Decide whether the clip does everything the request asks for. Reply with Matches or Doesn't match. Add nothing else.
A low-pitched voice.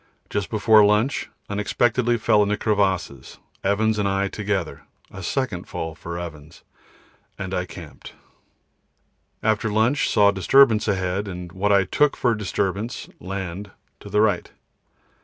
Matches